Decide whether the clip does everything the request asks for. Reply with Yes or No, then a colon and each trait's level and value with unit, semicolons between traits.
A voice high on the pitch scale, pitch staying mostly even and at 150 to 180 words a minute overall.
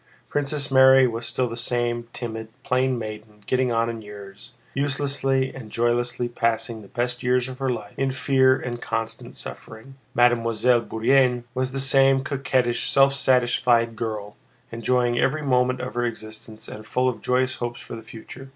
No: low, 120 Hz; narrow, 2.3 semitones; average, 165 wpm